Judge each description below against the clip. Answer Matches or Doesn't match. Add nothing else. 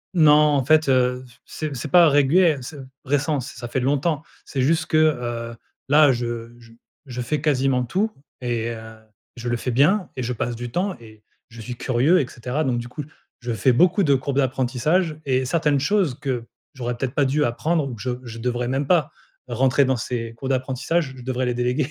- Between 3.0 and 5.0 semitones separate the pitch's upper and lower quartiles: Matches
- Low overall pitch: Matches